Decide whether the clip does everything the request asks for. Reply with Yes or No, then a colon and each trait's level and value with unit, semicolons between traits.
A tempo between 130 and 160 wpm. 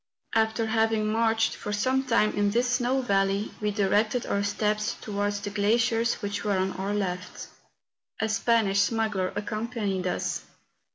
Yes: average, 155 wpm